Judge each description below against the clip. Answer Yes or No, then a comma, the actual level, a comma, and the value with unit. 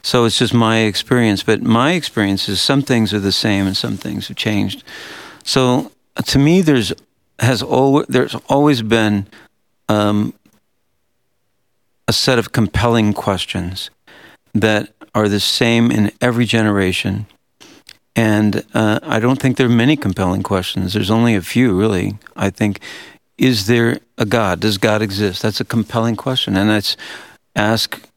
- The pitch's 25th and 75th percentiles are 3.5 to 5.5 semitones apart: No, average, 2.9 semitones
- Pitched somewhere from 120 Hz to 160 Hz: No, low, 110 Hz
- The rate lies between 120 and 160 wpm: Yes, average, 155 wpm